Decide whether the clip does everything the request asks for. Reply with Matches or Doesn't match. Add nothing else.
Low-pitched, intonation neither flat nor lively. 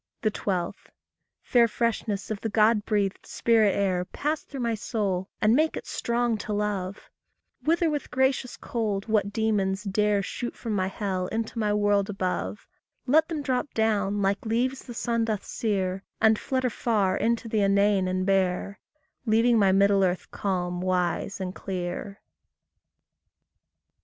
Doesn't match